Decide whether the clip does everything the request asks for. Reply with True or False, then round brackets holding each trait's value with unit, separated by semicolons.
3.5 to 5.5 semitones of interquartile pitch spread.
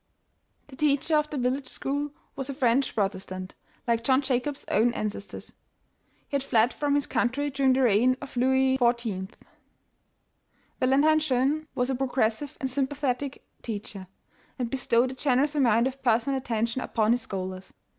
False (3.1 semitones)